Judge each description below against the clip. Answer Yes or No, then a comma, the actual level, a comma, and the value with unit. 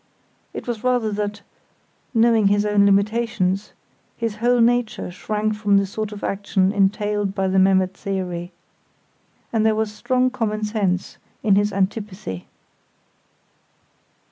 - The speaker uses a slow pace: Yes, slow, 130 wpm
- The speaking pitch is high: Yes, high, 210 Hz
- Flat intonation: Yes, narrow, 2.0 semitones